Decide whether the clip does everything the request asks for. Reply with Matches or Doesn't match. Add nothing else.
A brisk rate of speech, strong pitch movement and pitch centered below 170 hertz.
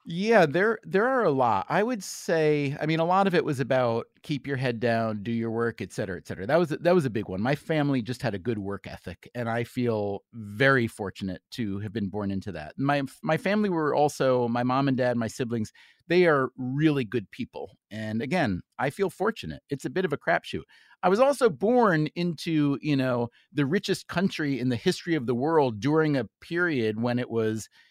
Matches